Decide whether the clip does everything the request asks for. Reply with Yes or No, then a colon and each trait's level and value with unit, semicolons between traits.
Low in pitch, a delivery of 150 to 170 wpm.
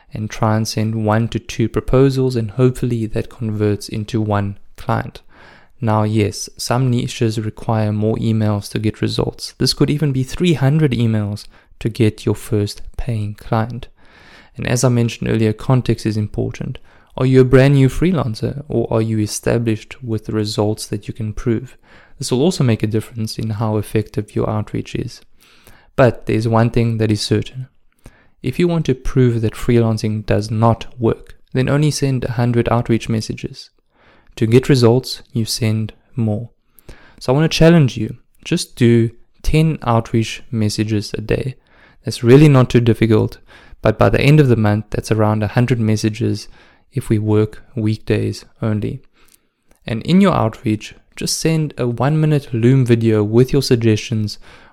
Yes: low, 115 Hz; average, 165 wpm